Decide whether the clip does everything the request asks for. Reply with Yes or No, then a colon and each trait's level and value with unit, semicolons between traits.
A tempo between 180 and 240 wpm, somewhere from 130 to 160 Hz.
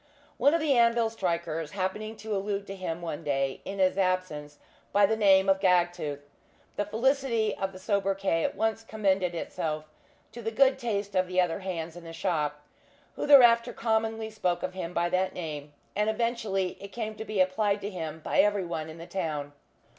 No: average, 190 wpm; high, 195 Hz